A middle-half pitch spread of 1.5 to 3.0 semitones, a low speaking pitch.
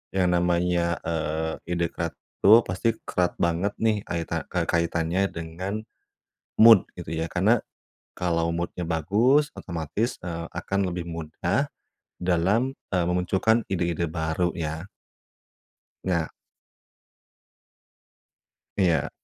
Yes: narrow, 2.5 semitones; very low, 85 Hz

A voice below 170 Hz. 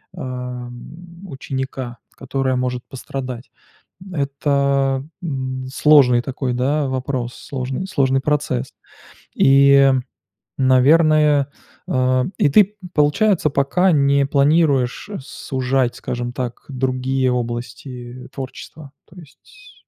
Yes: low, 135 Hz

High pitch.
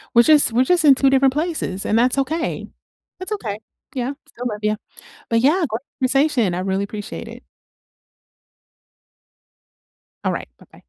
Yes: very high, 255 Hz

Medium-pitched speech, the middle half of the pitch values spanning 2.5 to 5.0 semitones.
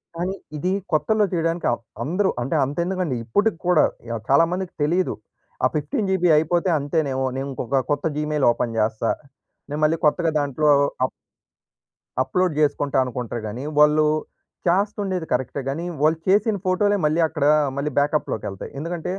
Yes: medium, 155 Hz; average, 4.5 semitones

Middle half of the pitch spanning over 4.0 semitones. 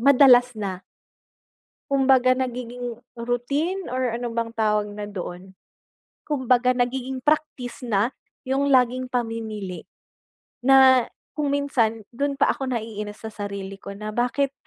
No: average, 3.5 semitones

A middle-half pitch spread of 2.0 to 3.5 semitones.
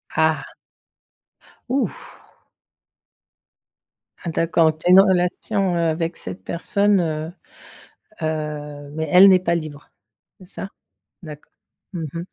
Yes: average, 2.7 semitones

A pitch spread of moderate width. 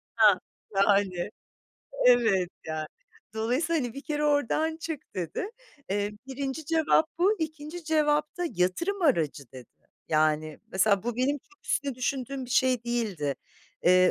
No: wide, 8.2 semitones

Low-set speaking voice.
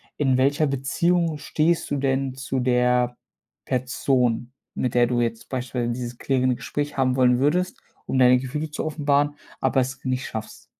Yes: low, 130 Hz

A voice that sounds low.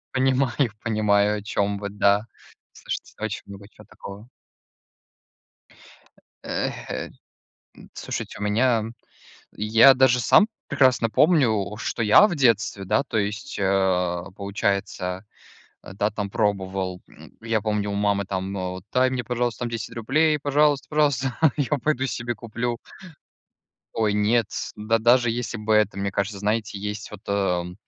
Yes: low, 105 Hz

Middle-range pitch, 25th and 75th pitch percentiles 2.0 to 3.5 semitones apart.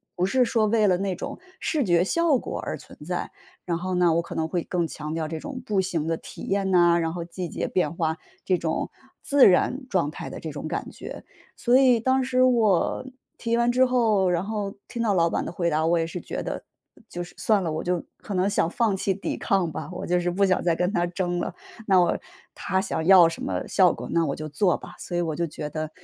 No: medium, 180 Hz; average, 3.9 semitones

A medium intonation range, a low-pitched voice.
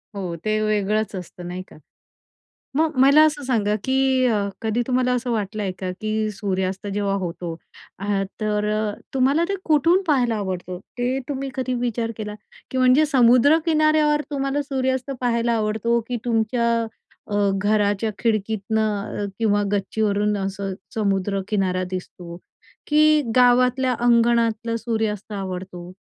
No: average, 4.1 semitones; high, 220 Hz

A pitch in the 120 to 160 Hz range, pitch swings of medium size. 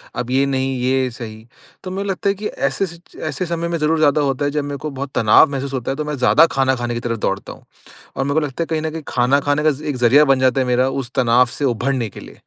Yes: low, 135 Hz; average, 3.2 semitones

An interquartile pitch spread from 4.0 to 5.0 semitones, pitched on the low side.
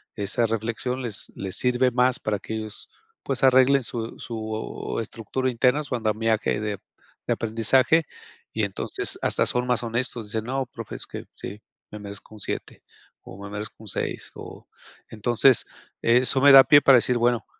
No: average, 2.8 semitones; low, 115 Hz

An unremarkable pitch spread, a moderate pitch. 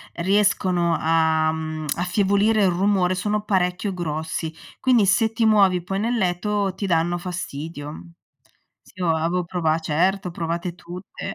Yes: average, 3.2 semitones; medium, 180 Hz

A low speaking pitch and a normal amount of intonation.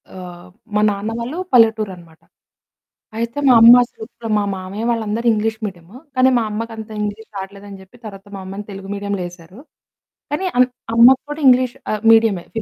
No: high, 215 Hz; average, 3.2 semitones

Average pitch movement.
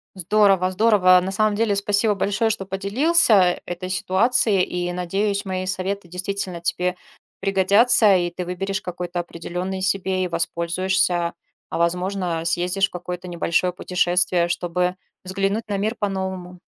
No: narrow, 1.9 semitones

